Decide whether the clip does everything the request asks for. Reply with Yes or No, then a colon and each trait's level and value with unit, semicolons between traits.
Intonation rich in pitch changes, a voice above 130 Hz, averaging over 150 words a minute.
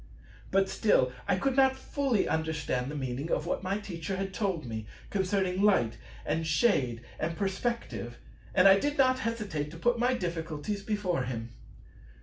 Yes: wide, 5.9 semitones; medium, 185 Hz; average, 160 wpm